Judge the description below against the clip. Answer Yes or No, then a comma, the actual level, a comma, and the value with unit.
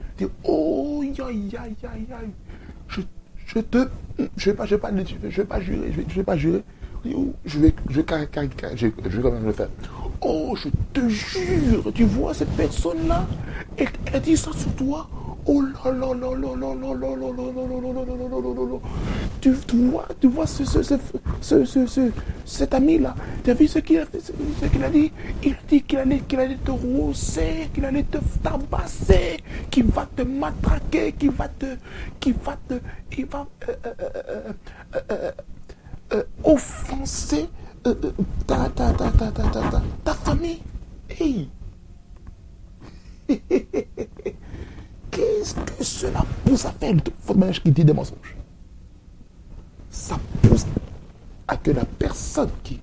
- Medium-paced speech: No, slow, 130 wpm